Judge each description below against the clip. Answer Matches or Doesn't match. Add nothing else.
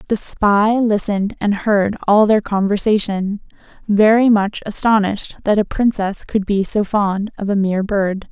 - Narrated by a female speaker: Matches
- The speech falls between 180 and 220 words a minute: Doesn't match